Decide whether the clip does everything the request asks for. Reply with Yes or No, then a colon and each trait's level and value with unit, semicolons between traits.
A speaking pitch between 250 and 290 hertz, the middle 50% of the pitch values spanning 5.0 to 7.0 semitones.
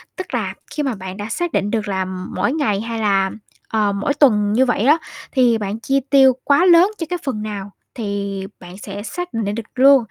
No: high, 220 Hz; average, 5.3 semitones